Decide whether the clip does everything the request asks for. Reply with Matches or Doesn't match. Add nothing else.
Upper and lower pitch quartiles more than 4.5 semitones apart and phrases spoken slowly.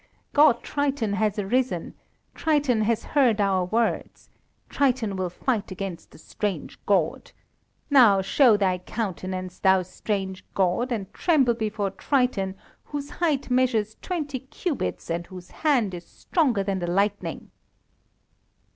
Matches